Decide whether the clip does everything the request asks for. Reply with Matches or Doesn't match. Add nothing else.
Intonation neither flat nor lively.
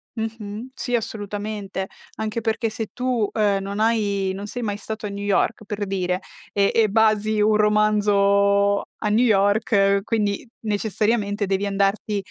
Doesn't match